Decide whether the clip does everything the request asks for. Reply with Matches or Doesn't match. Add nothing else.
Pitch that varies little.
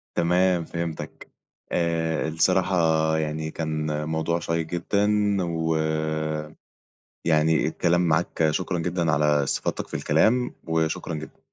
Matches